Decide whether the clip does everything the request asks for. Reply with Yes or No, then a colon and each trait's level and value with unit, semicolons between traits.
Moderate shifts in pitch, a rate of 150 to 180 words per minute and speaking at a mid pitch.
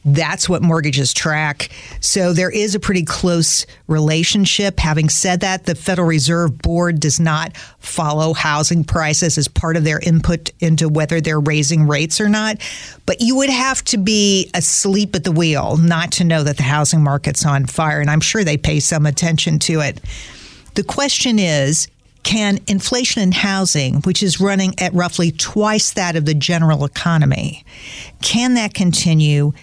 Yes: average, 3.8 semitones; average, 170 wpm; medium, 165 Hz